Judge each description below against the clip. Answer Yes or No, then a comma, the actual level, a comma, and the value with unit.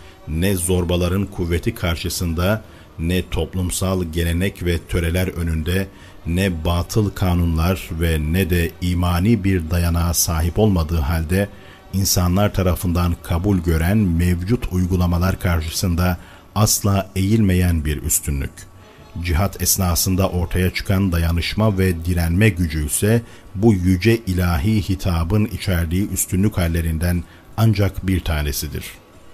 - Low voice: Yes, very low, 90 Hz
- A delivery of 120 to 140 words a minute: No, average, 105 wpm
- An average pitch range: No, narrow, 2.1 semitones